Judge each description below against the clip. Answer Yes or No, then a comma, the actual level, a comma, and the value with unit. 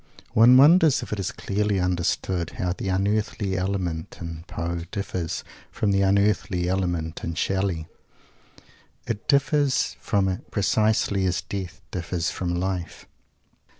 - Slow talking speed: Yes, slow, 130 wpm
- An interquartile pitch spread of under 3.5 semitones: Yes, average, 2.8 semitones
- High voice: No, very low, 95 Hz